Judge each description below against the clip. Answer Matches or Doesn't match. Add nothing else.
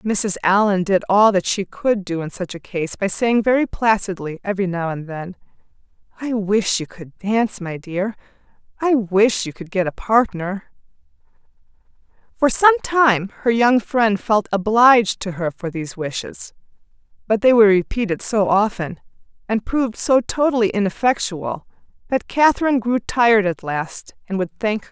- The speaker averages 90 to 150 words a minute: Doesn't match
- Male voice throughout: Doesn't match